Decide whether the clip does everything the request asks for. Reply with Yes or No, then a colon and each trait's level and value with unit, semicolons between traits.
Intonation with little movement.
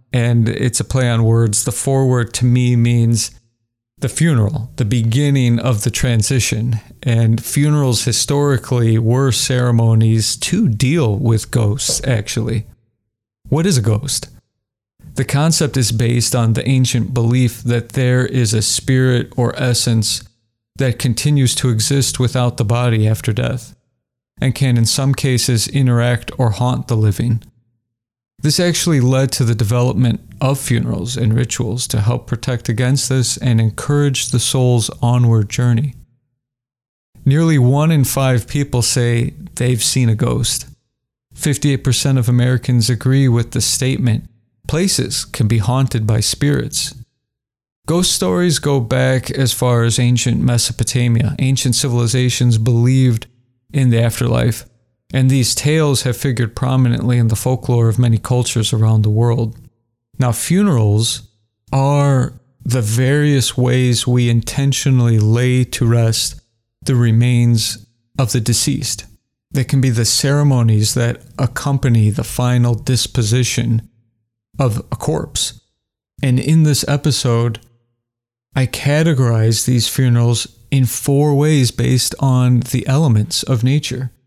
Yes: narrow, 2.3 semitones